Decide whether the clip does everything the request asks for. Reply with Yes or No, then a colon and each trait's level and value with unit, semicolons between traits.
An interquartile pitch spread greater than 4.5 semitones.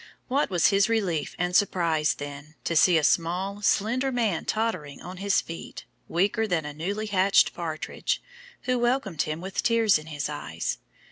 Yes: average, 5.2 semitones